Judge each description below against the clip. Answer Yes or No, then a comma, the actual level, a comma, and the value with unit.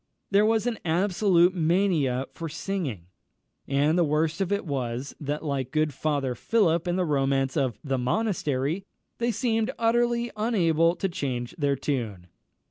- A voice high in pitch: No, medium, 160 Hz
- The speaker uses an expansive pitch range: Yes, wide, 6.3 semitones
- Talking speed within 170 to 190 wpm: No, average, 150 wpm